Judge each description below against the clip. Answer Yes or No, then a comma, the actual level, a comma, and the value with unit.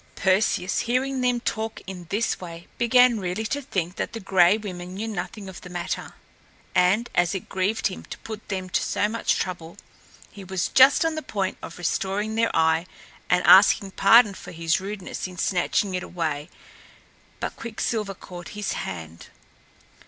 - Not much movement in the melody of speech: No, average, 3.7 semitones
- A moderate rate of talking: Yes, average, 170 wpm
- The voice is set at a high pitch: Yes, high, 195 Hz